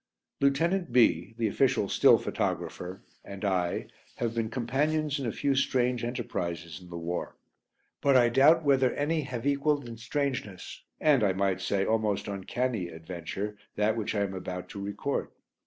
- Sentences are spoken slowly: No, average, 160 wpm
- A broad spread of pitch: Yes, wide, 6.0 semitones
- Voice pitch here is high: No, low, 115 Hz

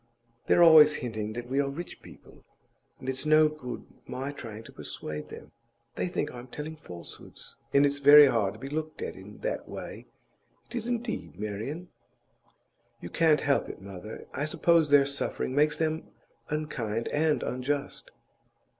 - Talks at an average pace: Yes, average, 165 wpm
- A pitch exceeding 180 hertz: No, medium, 140 Hz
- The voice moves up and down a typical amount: Yes, average, 4.3 semitones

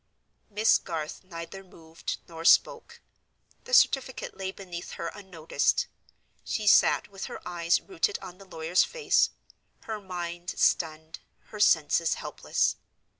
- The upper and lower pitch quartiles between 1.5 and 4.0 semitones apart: Yes, average, 3.5 semitones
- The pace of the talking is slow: Yes, slow, 125 wpm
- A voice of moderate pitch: Yes, medium, 180 Hz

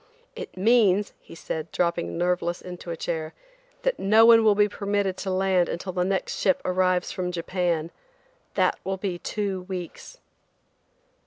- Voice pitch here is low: No, medium, 185 Hz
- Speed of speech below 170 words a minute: Yes, average, 155 wpm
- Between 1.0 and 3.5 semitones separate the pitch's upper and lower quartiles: Yes, narrow, 2.4 semitones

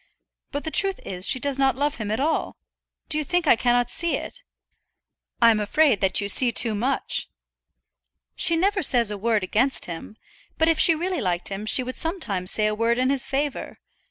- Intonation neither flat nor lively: No, wide, 6.5 semitones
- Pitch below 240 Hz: No, very high, 255 Hz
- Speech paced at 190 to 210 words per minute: Yes, average, 200 wpm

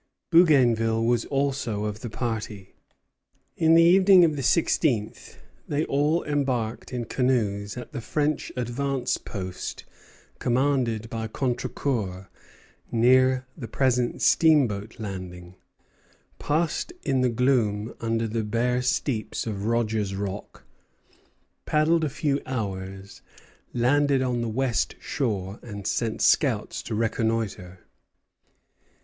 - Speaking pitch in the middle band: No, low, 120 Hz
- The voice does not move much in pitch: No, average, 4.3 semitones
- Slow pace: Yes, slow, 115 wpm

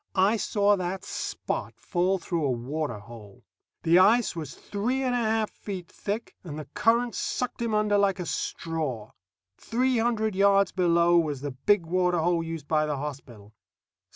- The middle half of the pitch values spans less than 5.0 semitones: No, wide, 5.4 semitones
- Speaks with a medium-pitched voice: Yes, medium, 180 Hz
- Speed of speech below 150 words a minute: No, average, 170 wpm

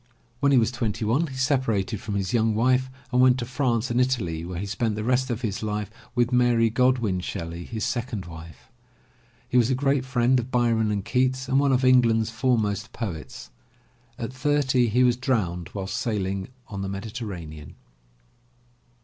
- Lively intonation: No, average, 4.0 semitones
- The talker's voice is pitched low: Yes, low, 115 Hz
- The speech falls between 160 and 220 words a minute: Yes, average, 180 wpm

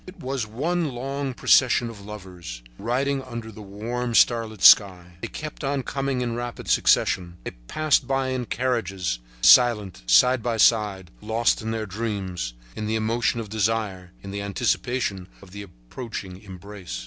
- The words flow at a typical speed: Yes, average, 160 wpm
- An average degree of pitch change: Yes, average, 4.2 semitones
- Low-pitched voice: Yes, low, 110 Hz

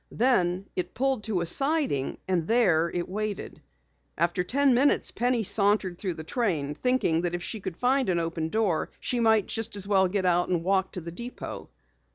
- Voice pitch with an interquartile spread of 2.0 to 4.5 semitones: No, average, 5.3 semitones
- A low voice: No, high, 190 Hz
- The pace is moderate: Yes, average, 180 wpm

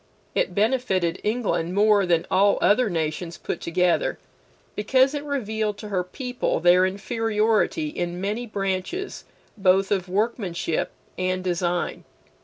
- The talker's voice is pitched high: Yes, high, 200 Hz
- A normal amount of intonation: Yes, average, 3.8 semitones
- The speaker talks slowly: Yes, slow, 125 wpm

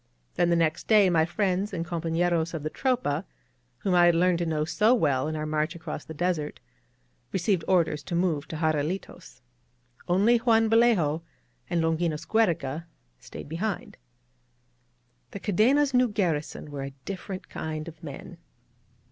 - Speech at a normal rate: Yes, average, 155 wpm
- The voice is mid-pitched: Yes, medium, 170 Hz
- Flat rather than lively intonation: No, average, 3.9 semitones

